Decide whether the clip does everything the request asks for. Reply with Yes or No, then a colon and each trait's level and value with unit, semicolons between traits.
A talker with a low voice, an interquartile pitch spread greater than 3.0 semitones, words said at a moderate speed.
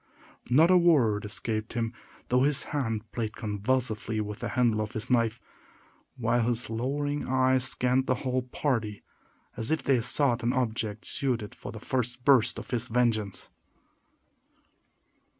No: low, 120 Hz; average, 2.7 semitones; average, 150 wpm